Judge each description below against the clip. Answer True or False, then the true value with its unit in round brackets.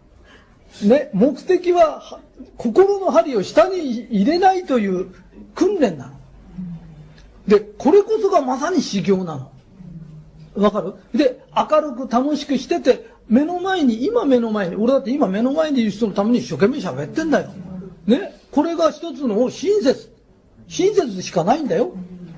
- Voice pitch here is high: True (245 Hz)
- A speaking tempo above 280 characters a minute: False (270 characters per minute)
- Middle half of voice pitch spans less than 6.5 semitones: False (7.9 semitones)